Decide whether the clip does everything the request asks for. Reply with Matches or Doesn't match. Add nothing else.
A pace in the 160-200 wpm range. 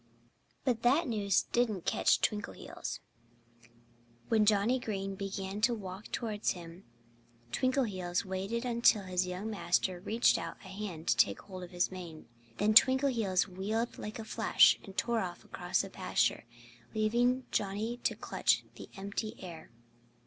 Doesn't match